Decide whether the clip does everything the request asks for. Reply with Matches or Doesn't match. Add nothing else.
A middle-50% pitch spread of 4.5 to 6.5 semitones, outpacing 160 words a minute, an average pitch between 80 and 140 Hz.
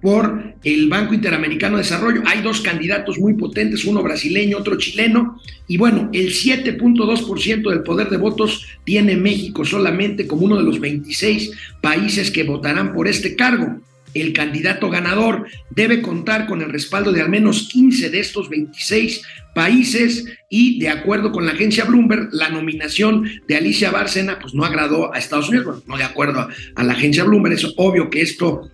Doesn't match